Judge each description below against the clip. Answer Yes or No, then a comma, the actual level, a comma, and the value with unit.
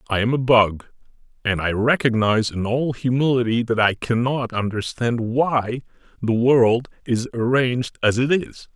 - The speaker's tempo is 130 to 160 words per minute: Yes, average, 150 wpm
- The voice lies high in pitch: No, low, 120 Hz